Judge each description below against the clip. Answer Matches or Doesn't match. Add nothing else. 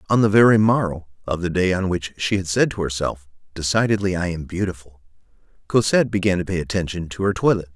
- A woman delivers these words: Doesn't match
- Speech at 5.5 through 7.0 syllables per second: Matches